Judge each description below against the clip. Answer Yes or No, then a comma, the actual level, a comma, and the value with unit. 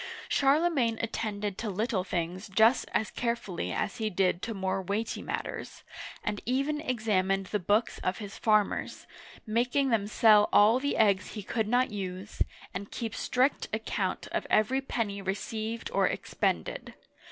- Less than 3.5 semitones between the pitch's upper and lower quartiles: Yes, average, 3.1 semitones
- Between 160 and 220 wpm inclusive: No, average, 150 wpm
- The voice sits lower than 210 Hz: No, high, 215 Hz